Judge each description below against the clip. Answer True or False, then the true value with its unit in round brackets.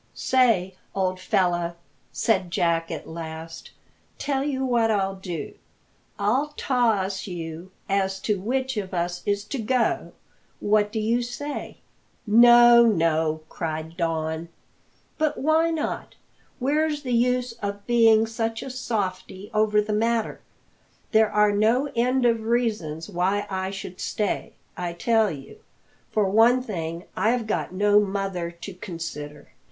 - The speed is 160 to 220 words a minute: False (135 wpm)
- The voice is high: True (210 Hz)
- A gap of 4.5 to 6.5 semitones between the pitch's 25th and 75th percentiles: True (5.0 semitones)